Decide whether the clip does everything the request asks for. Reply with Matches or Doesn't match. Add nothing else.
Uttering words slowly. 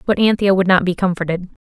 Doesn't match